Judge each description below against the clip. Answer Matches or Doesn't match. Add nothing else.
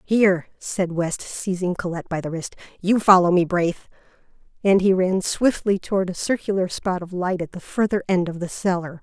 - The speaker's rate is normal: Matches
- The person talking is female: Matches